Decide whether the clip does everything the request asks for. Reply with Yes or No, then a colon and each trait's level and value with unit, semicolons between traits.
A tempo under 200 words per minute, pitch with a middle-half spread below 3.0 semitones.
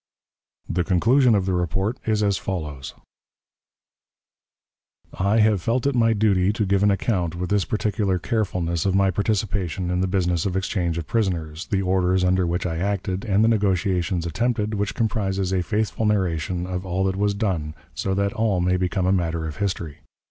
Yes: average, 180 wpm; narrow, 2.6 semitones